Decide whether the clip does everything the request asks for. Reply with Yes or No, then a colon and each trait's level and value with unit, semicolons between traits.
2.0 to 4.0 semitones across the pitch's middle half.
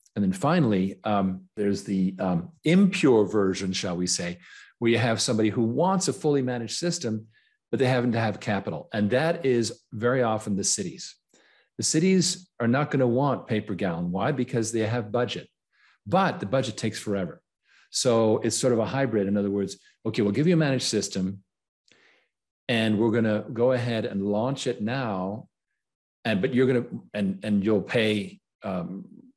No: average, 4.5 semitones